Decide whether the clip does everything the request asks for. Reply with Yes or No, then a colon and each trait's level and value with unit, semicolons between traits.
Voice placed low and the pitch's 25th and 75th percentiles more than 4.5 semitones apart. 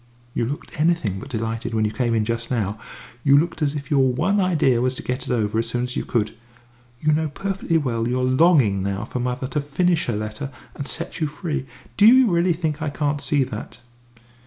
Yes: low, 130 Hz; average, 5.1 semitones